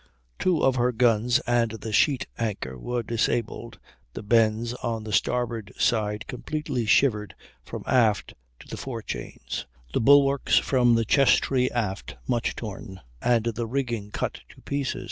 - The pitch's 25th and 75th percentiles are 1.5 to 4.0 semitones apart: Yes, narrow, 2.5 semitones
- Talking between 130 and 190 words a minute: Yes, average, 150 wpm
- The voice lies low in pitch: Yes, low, 115 Hz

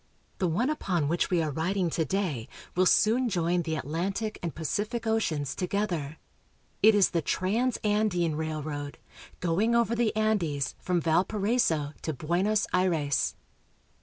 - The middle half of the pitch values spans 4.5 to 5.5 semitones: Yes, average, 5.1 semitones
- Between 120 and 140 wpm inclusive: Yes, slow, 135 wpm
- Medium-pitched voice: Yes, medium, 180 Hz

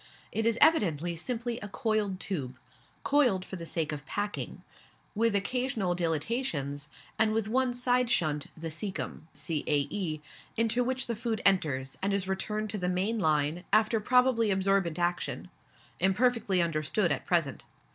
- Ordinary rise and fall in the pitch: No, wide, 5.7 semitones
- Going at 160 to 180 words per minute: No, average, 145 wpm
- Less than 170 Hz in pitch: No, high, 195 Hz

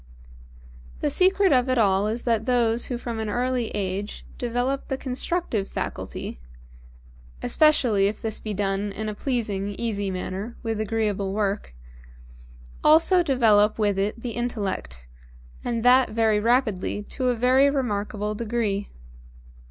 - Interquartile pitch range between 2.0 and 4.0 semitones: Yes, average, 3.4 semitones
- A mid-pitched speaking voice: No, high, 225 Hz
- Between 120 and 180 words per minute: Yes, slow, 135 wpm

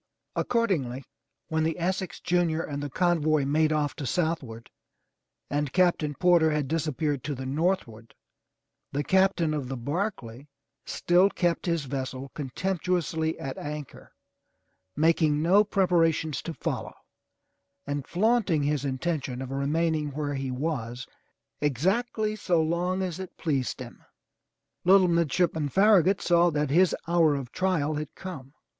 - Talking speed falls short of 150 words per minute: Yes, average, 140 wpm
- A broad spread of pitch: No, average, 3.9 semitones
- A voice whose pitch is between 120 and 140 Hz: No, medium, 155 Hz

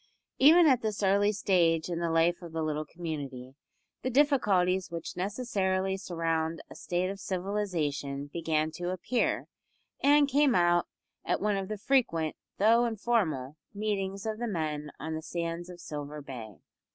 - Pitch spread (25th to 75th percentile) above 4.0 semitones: Yes, average, 4.6 semitones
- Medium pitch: Yes, medium, 180 Hz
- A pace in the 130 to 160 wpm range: Yes, average, 155 wpm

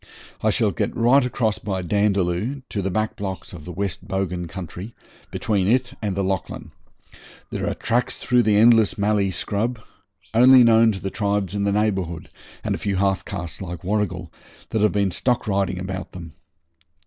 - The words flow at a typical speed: Yes, average, 180 wpm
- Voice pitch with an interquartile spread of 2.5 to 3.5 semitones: Yes, average, 2.8 semitones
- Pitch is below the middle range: Yes, low, 100 Hz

